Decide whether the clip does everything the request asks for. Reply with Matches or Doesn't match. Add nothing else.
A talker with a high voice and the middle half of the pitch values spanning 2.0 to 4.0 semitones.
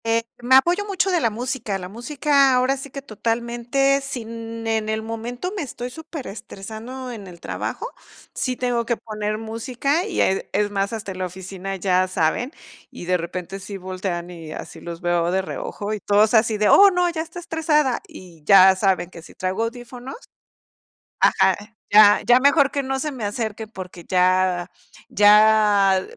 Doesn't match